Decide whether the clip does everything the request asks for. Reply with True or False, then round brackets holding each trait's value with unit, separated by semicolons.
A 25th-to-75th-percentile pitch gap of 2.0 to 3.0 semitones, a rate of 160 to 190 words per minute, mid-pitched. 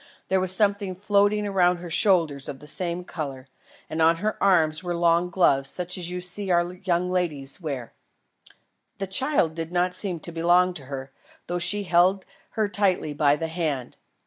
True (2.7 semitones; 180 wpm; 175 Hz)